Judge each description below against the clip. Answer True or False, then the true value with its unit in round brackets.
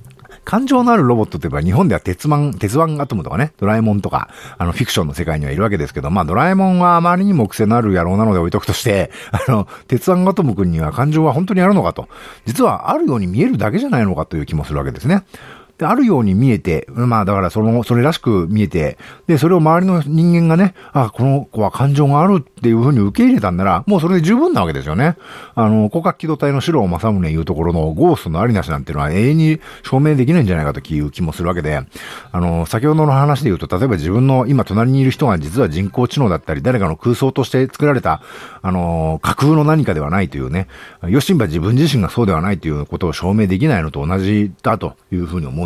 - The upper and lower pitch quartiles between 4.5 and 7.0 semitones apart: False (8.9 semitones)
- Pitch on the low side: True (115 Hz)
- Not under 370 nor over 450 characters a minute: False (485 characters per minute)